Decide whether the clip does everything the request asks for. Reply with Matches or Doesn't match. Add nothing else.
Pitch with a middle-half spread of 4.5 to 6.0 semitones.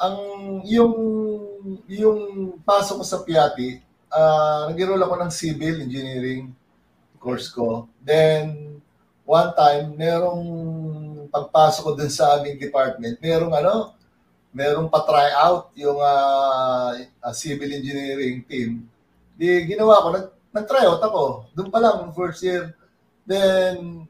Matches